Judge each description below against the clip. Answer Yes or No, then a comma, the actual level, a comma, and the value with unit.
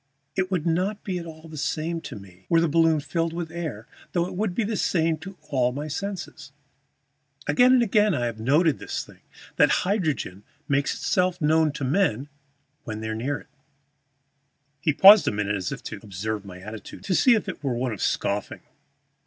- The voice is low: No, medium, 155 Hz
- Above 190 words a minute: Yes, average, 200 wpm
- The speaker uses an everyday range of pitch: No, wide, 6.9 semitones